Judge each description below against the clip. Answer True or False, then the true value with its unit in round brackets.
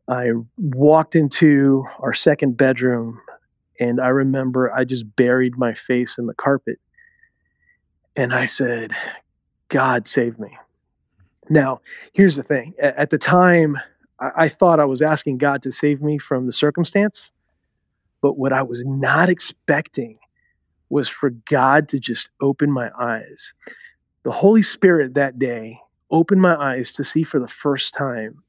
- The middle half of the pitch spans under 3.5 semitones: False (3.9 semitones)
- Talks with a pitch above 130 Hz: True (140 Hz)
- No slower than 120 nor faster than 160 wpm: True (145 wpm)